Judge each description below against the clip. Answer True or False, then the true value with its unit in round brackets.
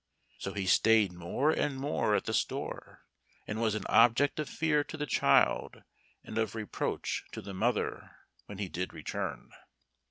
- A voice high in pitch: False (110 Hz)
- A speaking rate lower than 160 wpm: False (165 wpm)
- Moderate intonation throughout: False (6.1 semitones)